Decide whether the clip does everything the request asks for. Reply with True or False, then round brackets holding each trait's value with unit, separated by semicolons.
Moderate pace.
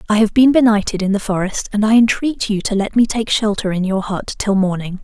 False (250 wpm)